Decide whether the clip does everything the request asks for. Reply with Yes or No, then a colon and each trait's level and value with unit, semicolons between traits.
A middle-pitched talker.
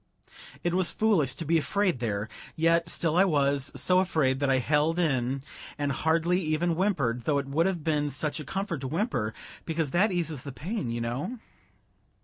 Yes: medium, 155 Hz